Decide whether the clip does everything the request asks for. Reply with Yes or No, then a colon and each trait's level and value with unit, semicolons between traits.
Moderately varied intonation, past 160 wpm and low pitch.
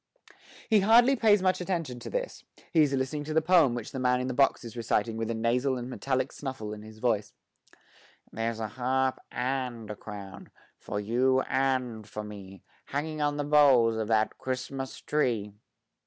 Yes: average, 4.4 semitones; average, 185 wpm; low, 130 Hz